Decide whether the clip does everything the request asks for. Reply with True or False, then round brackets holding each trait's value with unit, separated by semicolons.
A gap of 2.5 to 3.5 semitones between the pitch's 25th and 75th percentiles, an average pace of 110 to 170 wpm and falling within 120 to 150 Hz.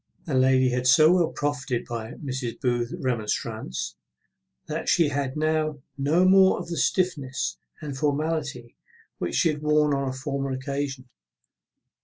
True (3.0 semitones; 145 wpm; 140 Hz)